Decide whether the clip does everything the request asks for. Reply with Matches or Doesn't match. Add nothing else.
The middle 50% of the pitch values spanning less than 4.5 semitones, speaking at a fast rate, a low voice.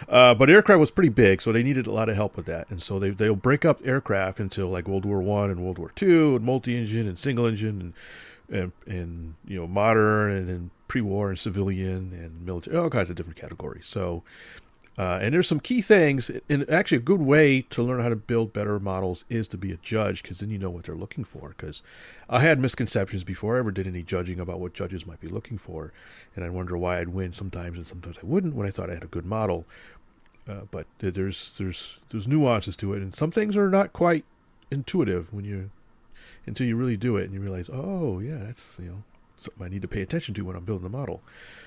Doesn't match